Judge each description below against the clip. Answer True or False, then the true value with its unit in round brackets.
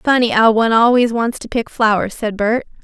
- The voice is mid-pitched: False (230 Hz)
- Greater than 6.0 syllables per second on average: False (5.5 syllables/s)